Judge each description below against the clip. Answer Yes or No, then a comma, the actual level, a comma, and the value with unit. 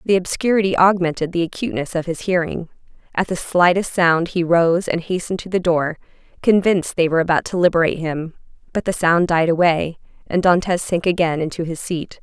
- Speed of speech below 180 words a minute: No, average, 185 wpm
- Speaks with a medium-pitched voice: Yes, medium, 175 Hz